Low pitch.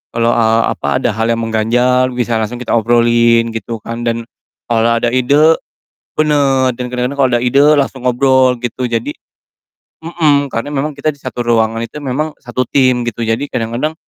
Yes: low, 120 Hz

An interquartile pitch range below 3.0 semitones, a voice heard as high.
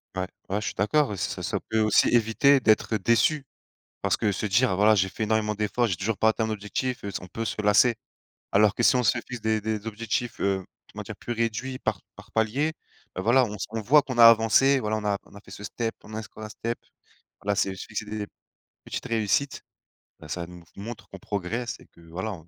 No: narrow, 2.5 semitones; low, 110 Hz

